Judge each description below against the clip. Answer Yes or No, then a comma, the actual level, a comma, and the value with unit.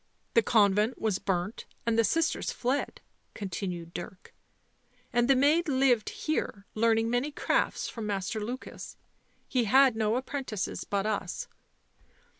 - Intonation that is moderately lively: Yes, average, 4.3 semitones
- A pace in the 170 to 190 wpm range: No, slow, 135 wpm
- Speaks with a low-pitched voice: No, high, 225 Hz